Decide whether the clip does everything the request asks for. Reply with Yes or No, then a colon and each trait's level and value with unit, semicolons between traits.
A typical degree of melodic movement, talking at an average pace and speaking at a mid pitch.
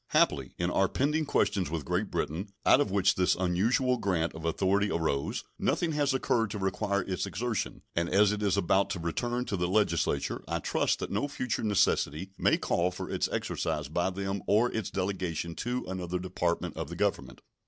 No: average, 3.7 semitones; average, 190 wpm; very low, 95 Hz